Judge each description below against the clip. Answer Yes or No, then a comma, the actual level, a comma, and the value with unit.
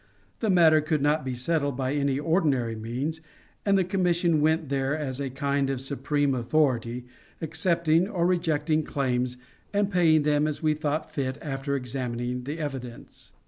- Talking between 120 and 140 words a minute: No, average, 160 wpm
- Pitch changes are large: No, average, 3.3 semitones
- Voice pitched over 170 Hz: No, medium, 145 Hz